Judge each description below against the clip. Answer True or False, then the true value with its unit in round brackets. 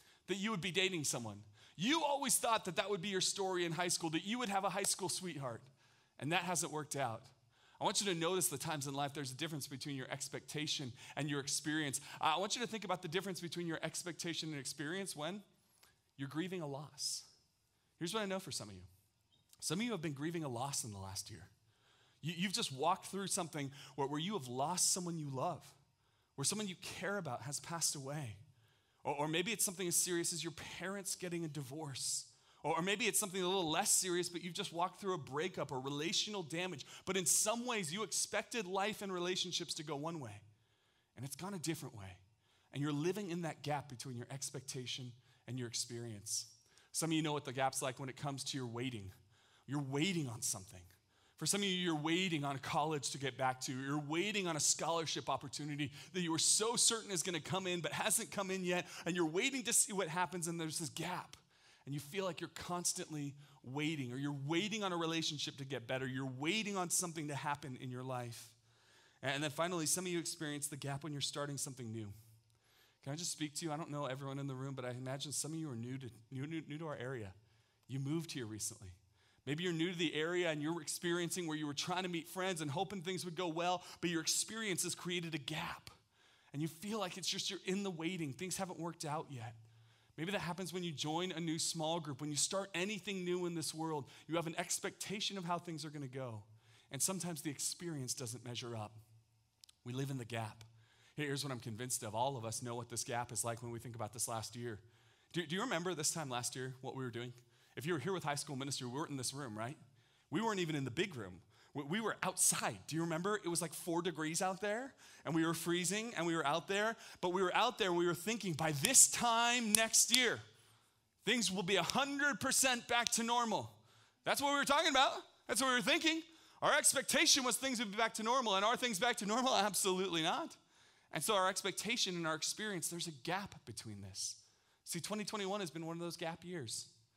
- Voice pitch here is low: False (160 Hz)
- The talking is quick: True (235 wpm)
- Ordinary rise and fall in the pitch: False (5.8 semitones)